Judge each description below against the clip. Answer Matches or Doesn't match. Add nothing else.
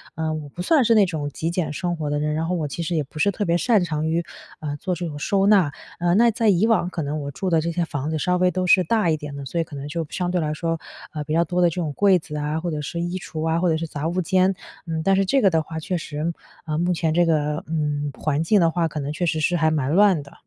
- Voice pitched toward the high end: Doesn't match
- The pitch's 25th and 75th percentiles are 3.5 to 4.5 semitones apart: Doesn't match